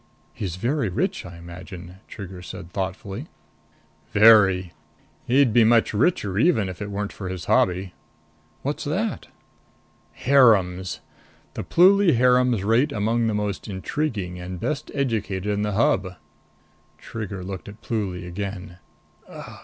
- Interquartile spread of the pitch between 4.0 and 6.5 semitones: Yes, average, 4.3 semitones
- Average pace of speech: No, slow, 130 wpm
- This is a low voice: Yes, low, 100 Hz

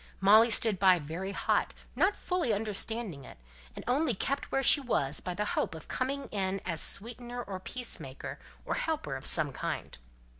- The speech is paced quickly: No, average, 175 wpm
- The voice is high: Yes, high, 210 Hz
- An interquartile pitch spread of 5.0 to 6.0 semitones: Yes, wide, 5.5 semitones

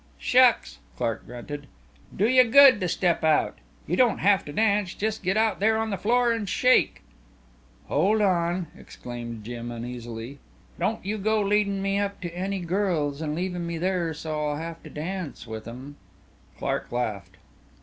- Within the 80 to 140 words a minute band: No, average, 170 wpm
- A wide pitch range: Yes, wide, 6.1 semitones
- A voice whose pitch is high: No, medium, 180 Hz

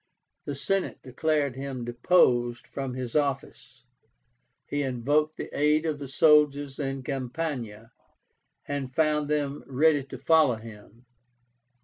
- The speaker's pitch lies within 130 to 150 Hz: Yes, medium, 140 Hz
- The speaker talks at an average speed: No, slow, 120 wpm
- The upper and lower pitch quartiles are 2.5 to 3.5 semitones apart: Yes, average, 3.1 semitones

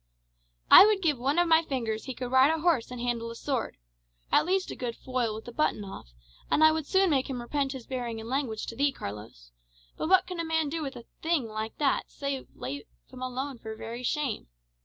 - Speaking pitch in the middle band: No, very high, 260 Hz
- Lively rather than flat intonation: No, average, 5.0 semitones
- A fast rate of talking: Yes, fast, 235 wpm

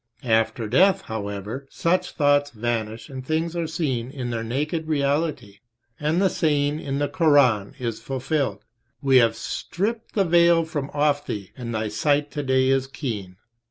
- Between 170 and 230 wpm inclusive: No, average, 160 wpm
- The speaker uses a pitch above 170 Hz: No, medium, 140 Hz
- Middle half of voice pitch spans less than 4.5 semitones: No, average, 5.2 semitones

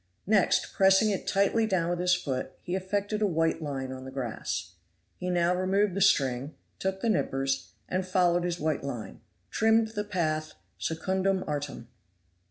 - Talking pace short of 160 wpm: No, average, 165 wpm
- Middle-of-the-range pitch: Yes, medium, 180 Hz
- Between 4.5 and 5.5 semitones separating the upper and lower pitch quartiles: Yes, average, 4.9 semitones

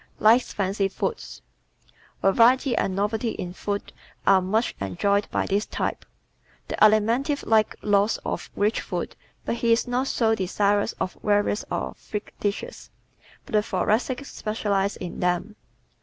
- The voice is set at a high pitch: Yes, high, 210 Hz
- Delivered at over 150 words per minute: No, average, 145 wpm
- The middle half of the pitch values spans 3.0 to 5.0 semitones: No, narrow, 2.6 semitones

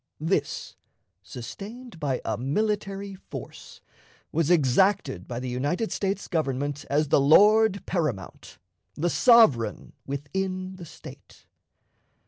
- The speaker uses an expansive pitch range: Yes, wide, 6.3 semitones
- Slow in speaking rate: Yes, slow, 110 wpm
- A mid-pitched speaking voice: Yes, medium, 165 Hz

